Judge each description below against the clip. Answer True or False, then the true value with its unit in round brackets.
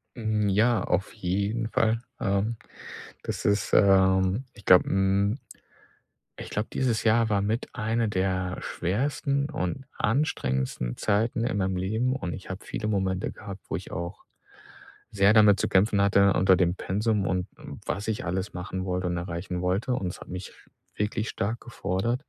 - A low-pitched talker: True (100 Hz)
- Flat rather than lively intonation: False (3.1 semitones)